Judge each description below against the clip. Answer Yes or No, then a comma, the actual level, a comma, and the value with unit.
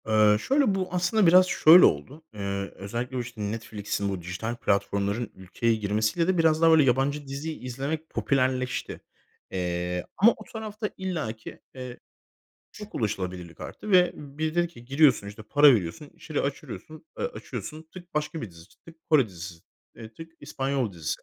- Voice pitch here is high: No, low, 130 Hz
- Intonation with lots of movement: Yes, wide, 7.6 semitones